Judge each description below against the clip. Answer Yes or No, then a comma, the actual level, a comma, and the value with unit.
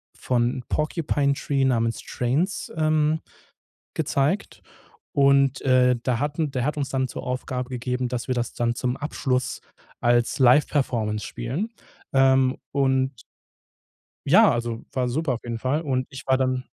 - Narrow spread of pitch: Yes, narrow, 2.2 semitones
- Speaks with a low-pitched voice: Yes, low, 130 Hz